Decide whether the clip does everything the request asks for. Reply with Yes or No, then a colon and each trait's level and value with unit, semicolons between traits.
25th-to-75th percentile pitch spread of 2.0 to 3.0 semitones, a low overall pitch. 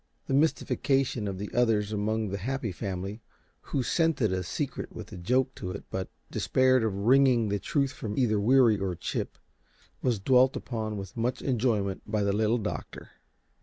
No: average, 4.3 semitones; low, 110 Hz